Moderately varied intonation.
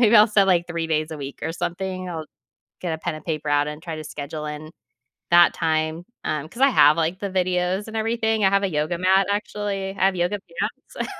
Yes: average, 3.8 semitones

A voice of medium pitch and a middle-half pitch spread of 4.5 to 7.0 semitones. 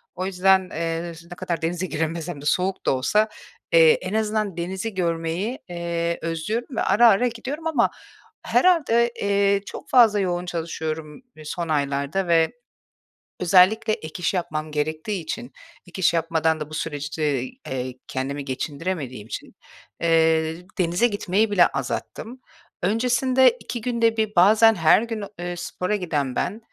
Yes: medium, 180 Hz; average, 5.2 semitones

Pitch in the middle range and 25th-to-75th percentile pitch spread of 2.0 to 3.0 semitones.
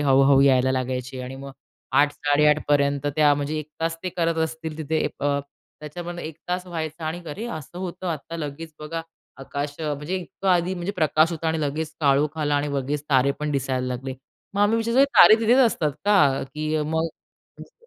Yes: medium, 150 Hz; average, 2.7 semitones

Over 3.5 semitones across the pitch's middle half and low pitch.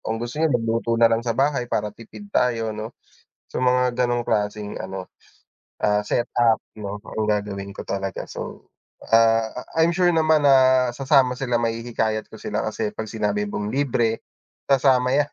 No: average, 3.2 semitones; low, 115 Hz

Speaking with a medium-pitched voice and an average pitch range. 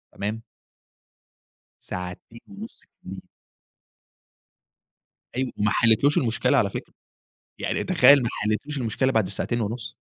No: low, 115 Hz; average, 3.9 semitones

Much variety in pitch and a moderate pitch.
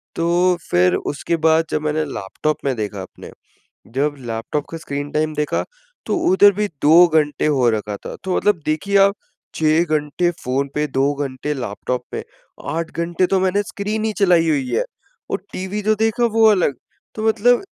Yes: wide, 5.8 semitones; medium, 155 Hz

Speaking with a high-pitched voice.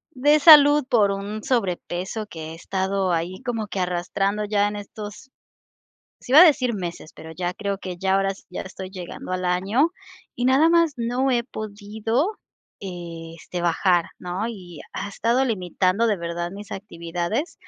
Yes: high, 200 Hz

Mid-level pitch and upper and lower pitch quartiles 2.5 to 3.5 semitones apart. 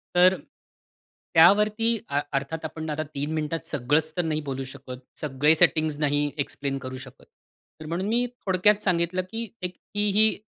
No: medium, 160 Hz; average, 4.2 semitones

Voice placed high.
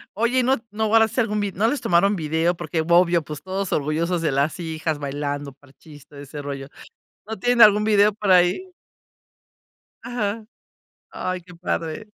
No: medium, 180 Hz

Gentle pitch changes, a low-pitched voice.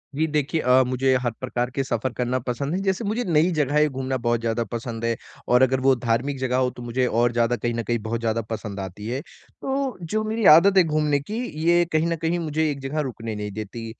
No: average, 4.8 semitones; low, 130 Hz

